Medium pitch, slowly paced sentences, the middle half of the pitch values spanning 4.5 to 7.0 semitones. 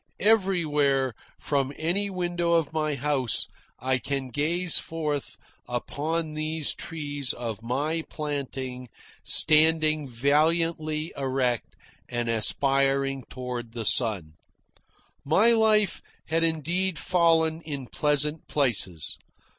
No: medium, 150 Hz; slow, 100 wpm; average, 3.8 semitones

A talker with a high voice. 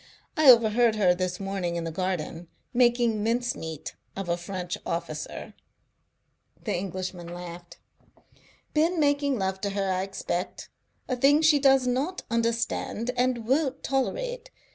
Yes: high, 215 Hz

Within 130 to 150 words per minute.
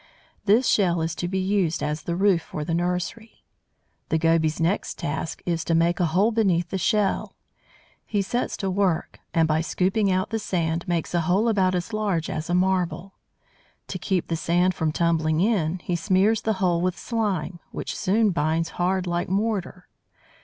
No: average, 180 wpm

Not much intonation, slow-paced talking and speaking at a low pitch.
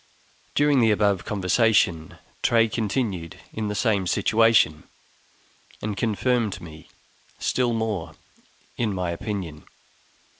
No: average, 3.8 semitones; slow, 105 wpm; low, 105 Hz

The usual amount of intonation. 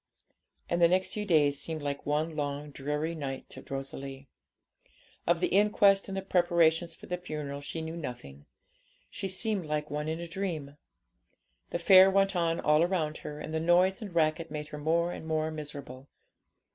Yes: average, 3.1 semitones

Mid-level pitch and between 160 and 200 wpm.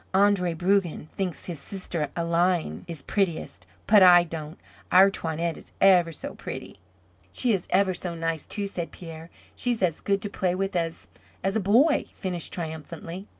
Yes: medium, 180 Hz; average, 165 wpm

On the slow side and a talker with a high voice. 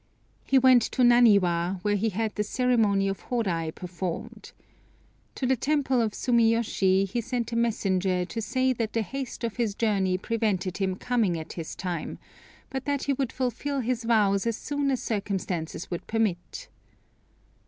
No: average, 165 wpm; high, 225 Hz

